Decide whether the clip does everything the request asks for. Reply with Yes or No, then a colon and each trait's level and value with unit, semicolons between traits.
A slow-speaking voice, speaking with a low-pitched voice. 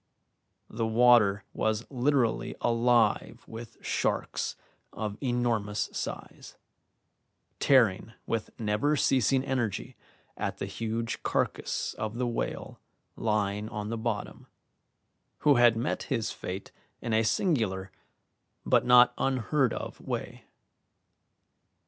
Yes: slow, 105 wpm; low, 115 Hz